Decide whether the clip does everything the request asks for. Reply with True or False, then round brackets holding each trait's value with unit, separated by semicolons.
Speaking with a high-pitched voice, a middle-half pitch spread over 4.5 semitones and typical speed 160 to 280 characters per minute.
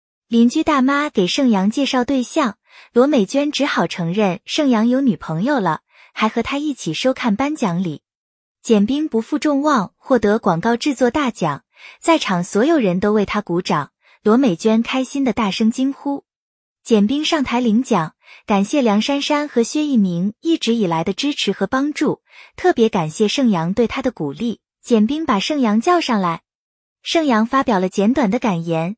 True (235 Hz; 5.5 semitones; 255 characters per minute)